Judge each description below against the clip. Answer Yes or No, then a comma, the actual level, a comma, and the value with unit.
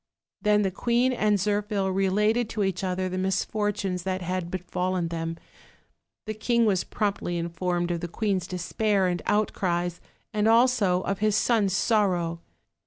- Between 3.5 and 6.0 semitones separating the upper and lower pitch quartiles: No, average, 2.8 semitones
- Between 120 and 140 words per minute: No, average, 150 wpm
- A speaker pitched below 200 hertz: Yes, high, 190 Hz